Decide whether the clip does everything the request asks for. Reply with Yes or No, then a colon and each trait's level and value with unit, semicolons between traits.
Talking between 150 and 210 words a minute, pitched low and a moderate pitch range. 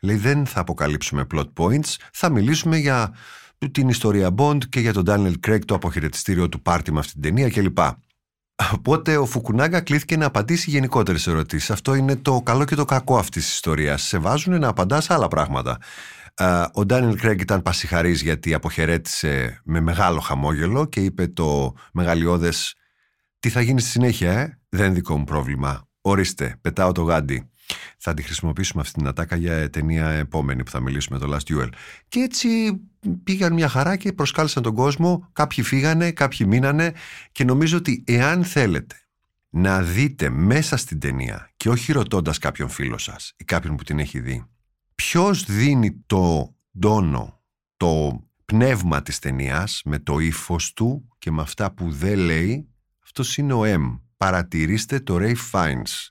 No: average, 165 wpm; very low, 95 Hz; wide, 9.0 semitones